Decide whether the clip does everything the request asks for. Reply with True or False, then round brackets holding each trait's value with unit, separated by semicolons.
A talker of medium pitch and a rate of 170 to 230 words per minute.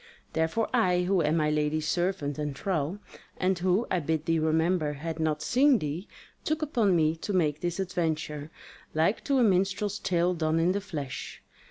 True (170 Hz; 180 wpm)